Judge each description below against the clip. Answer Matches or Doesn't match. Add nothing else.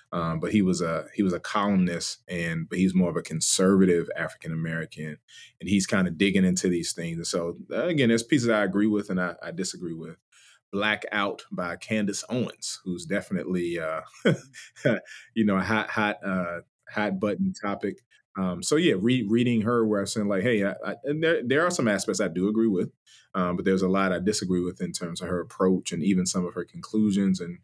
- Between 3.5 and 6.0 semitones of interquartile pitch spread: Doesn't match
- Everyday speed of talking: Doesn't match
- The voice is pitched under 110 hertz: Matches